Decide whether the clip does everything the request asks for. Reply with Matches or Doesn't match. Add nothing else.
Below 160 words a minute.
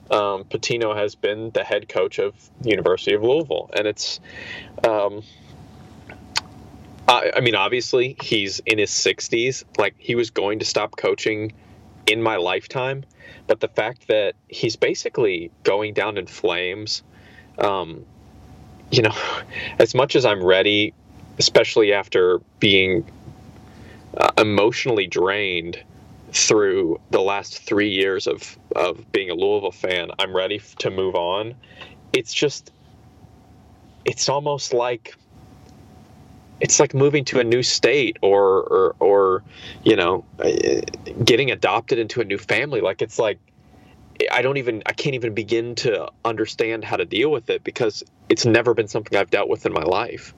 Matches